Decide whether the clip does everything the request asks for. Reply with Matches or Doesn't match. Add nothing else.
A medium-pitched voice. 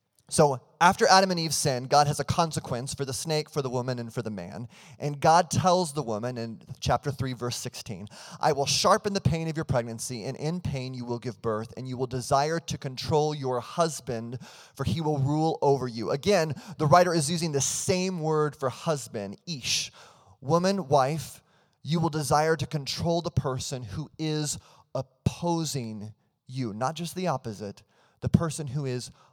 Matches